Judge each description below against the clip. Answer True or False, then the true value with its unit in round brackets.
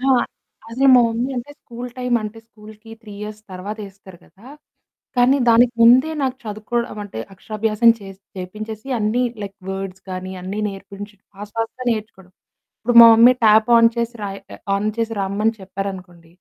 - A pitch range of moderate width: True (3.0 semitones)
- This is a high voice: True (215 Hz)